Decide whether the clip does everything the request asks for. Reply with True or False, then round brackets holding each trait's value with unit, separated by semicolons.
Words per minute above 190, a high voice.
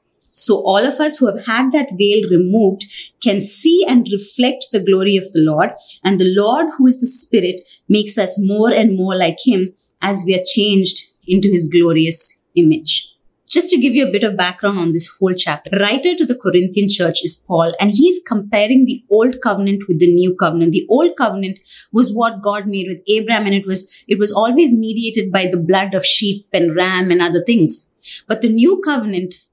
True (205 wpm; 200 Hz)